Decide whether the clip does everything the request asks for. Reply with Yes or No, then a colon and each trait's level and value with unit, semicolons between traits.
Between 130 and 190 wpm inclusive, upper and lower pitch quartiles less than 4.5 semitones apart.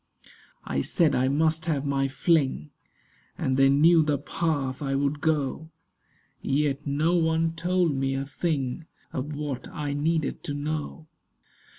Yes: average, 145 wpm; average, 2.8 semitones